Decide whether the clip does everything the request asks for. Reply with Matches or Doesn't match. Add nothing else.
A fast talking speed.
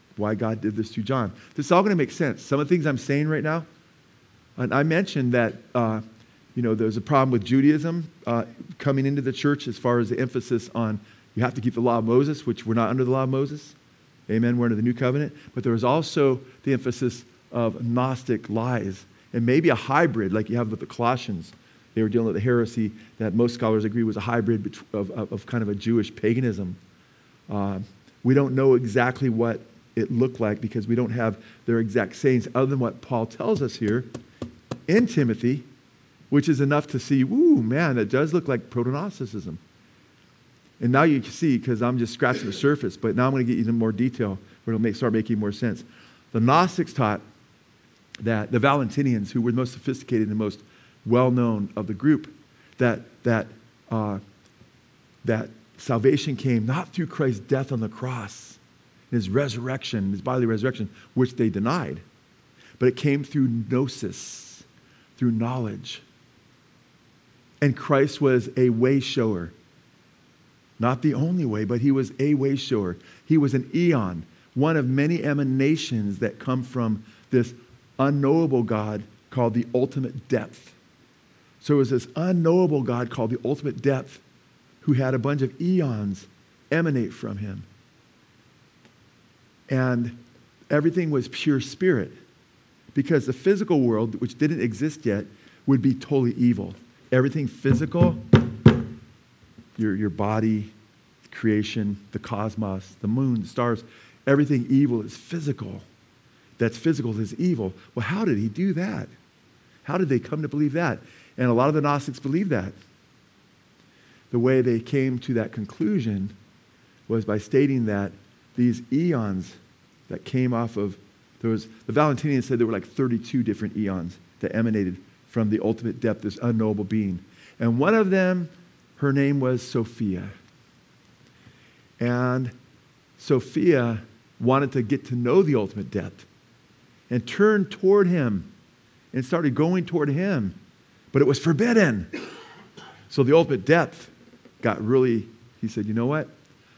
Doesn't match